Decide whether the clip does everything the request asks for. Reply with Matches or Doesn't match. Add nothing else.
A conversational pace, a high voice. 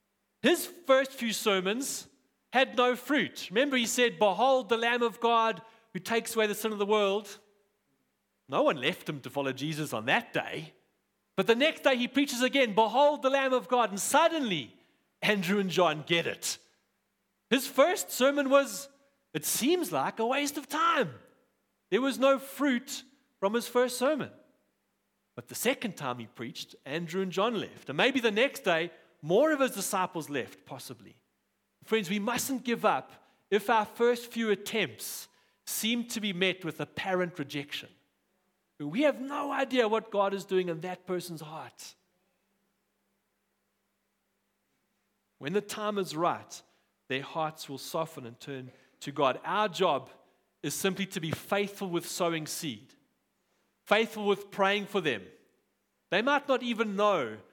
Matches